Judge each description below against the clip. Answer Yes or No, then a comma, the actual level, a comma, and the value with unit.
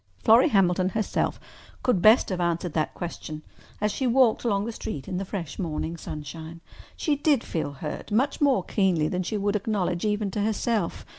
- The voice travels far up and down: No, average, 4.4 semitones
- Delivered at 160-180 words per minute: Yes, average, 175 wpm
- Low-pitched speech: No, high, 195 Hz